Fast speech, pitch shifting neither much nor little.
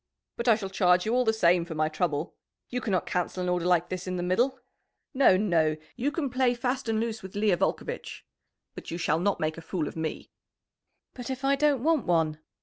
No: fast, 225 wpm; wide, 6.2 semitones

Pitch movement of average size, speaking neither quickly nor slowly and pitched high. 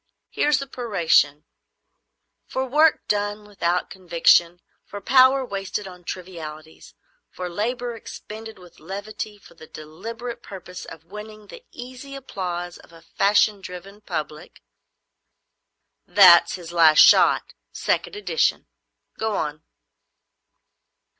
No: average, 4.6 semitones; slow, 115 wpm; high, 195 Hz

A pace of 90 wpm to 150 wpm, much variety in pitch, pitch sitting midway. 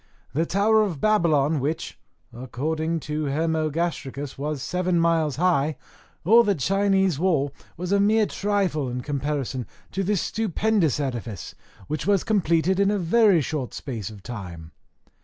Yes: average, 140 wpm; wide, 5.7 semitones; medium, 160 Hz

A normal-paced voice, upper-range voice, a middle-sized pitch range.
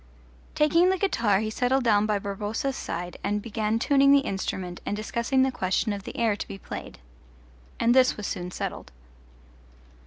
Yes: average, 175 wpm; high, 220 Hz; average, 4.6 semitones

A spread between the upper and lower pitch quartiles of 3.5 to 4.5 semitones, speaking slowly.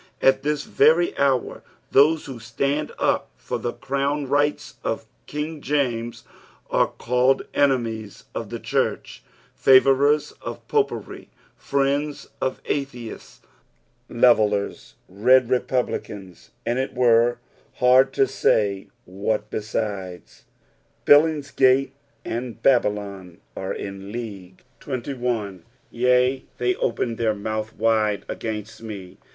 Yes: average, 4.2 semitones; slow, 110 wpm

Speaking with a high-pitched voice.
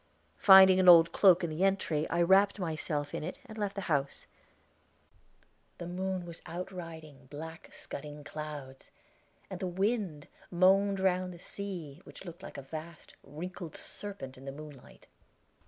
No: medium, 170 Hz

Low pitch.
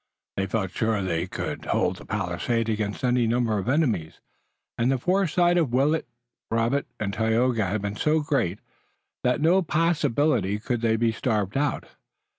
Yes: low, 115 Hz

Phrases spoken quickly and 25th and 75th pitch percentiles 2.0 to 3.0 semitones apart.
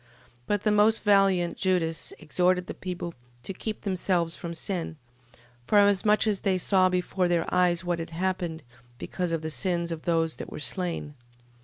No: average, 165 wpm; narrow, 2.4 semitones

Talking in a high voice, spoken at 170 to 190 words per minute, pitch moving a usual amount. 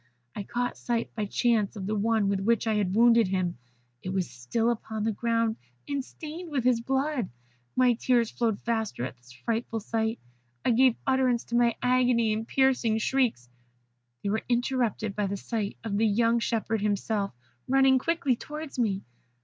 Yes: high, 230 Hz; average, 175 wpm; average, 3.0 semitones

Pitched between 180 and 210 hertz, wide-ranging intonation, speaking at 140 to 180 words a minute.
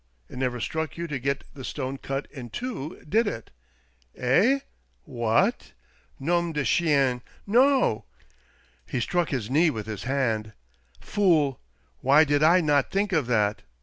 No: medium, 140 Hz; wide, 5.7 semitones; average, 150 wpm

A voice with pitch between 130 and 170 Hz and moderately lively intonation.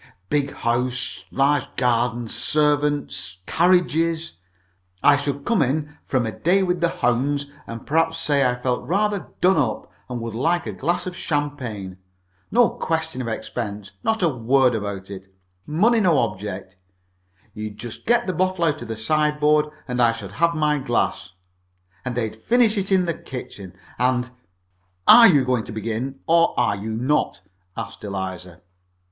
No: low, 135 Hz; wide, 6.3 semitones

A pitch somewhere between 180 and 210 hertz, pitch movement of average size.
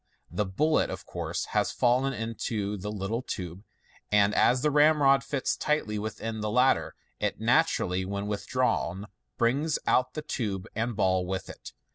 No: low, 110 Hz; average, 4.4 semitones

